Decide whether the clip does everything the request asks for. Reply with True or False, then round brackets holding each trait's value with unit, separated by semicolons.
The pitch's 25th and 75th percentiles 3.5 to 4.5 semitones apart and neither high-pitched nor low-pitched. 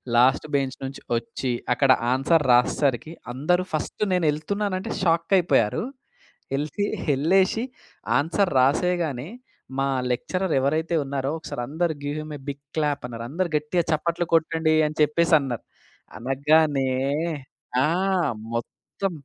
True (3.9 semitones; 150 Hz)